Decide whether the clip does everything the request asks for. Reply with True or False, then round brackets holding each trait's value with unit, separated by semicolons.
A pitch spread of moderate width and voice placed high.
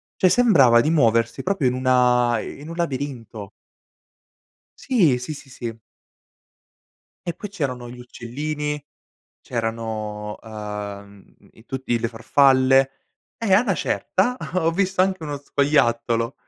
False (5.0 semitones; 130 Hz)